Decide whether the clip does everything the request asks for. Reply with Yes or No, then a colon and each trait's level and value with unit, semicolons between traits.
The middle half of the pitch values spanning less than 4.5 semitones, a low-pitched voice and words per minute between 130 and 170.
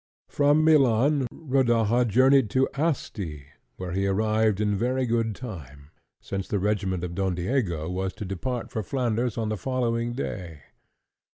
No: average, 5.0 semitones; low, 110 Hz; average, 150 wpm